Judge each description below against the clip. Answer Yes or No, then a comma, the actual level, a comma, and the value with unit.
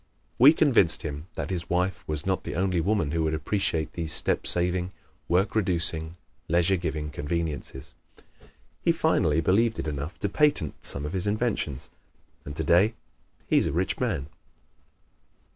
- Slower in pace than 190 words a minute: Yes, average, 155 wpm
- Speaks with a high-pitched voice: No, very low, 85 Hz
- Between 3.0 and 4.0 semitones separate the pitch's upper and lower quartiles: Yes, average, 3.7 semitones